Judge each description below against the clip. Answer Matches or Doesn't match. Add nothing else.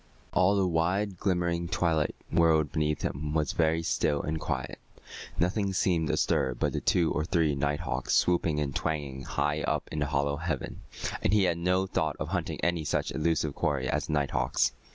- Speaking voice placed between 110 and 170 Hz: Doesn't match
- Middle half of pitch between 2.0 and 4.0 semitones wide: Matches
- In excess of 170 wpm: Matches